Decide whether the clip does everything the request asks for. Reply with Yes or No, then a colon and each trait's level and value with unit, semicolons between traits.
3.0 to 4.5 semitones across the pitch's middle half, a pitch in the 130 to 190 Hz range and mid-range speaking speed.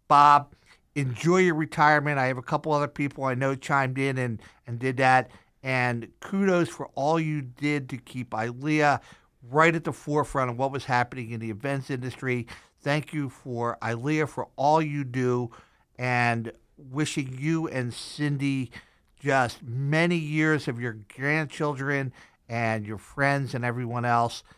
Yes: average, 3.3 semitones; low, 135 Hz; average, 155 wpm